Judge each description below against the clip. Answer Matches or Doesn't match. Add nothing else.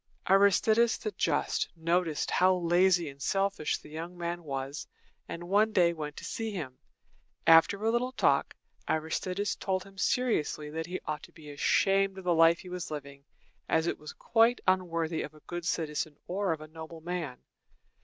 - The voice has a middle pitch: Matches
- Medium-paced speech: Matches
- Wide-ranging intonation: Doesn't match